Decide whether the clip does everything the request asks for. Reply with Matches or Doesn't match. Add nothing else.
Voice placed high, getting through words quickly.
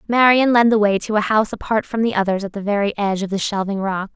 Matches